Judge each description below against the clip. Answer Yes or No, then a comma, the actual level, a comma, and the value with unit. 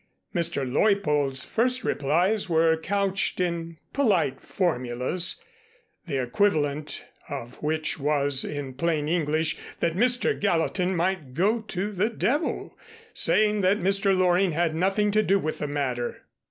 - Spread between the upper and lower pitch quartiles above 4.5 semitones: Yes, average, 5.1 semitones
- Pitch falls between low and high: Yes, medium, 170 Hz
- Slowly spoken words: Yes, slow, 130 wpm